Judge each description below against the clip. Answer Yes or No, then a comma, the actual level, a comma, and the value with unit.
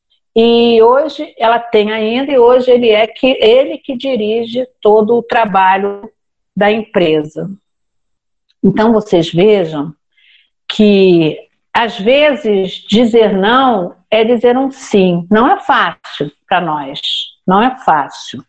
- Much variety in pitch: No, average, 4.2 semitones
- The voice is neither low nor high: No, high, 220 Hz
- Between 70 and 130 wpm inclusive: Yes, average, 125 wpm